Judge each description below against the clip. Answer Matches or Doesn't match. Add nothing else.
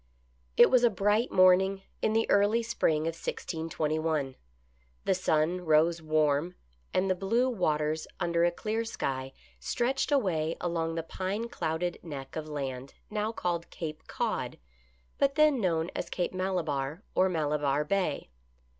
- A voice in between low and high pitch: Matches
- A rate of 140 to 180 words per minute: Matches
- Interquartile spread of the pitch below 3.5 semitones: Doesn't match